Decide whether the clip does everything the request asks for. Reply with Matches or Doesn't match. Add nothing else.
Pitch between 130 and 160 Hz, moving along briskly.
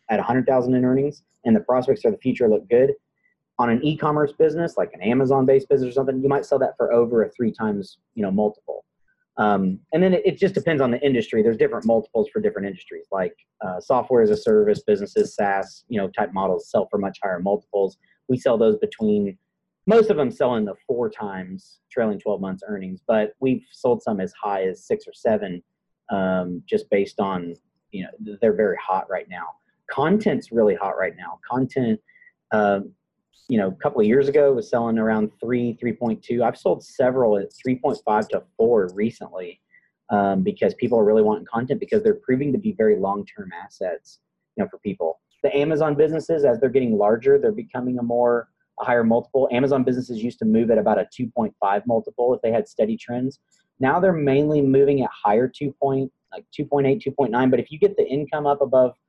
Matches